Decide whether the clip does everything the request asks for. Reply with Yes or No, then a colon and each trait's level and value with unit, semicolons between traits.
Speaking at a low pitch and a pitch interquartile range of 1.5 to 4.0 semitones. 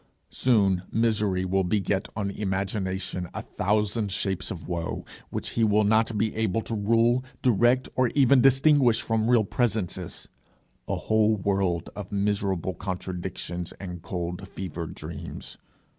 Yes: low, 100 Hz; average, 3.3 semitones